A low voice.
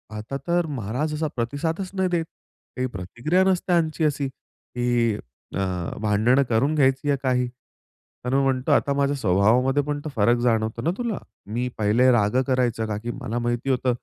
Yes: low, 130 Hz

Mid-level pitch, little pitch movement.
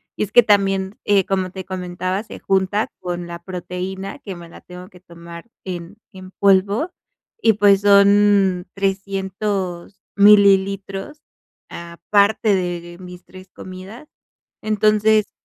No: high, 195 Hz; narrow, 2.0 semitones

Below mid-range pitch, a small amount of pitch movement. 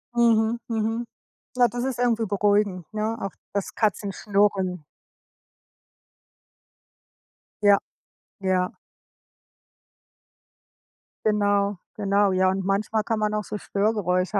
No: high, 205 Hz; narrow, 2.0 semitones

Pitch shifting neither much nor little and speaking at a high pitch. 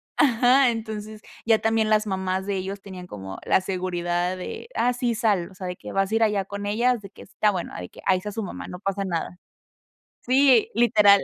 Yes: average, 3.2 semitones; high, 200 Hz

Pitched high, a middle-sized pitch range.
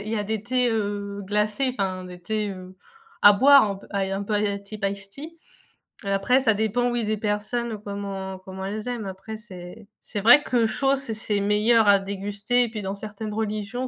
No: high, 210 Hz; narrow, 2.2 semitones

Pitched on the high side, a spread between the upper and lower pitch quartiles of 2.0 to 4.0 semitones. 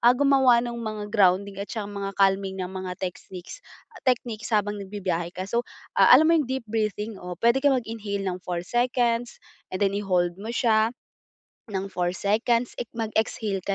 Yes: high, 210 Hz; average, 3.6 semitones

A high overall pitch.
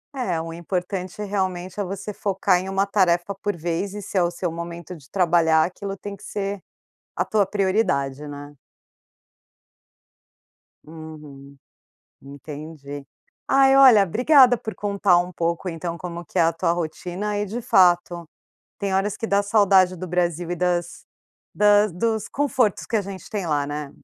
No: medium, 180 Hz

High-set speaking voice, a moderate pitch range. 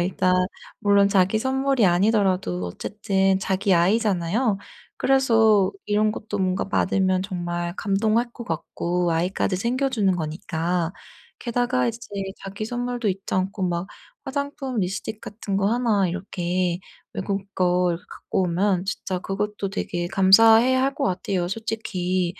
Yes: high, 195 Hz; average, 3.6 semitones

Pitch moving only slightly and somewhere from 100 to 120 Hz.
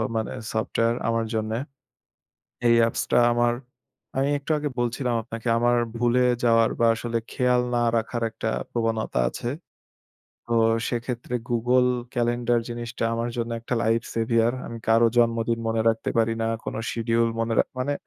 Yes: narrow, 1.0 semitones; low, 115 Hz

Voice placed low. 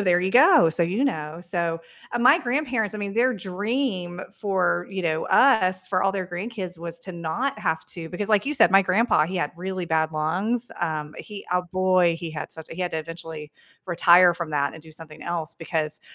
No: medium, 180 Hz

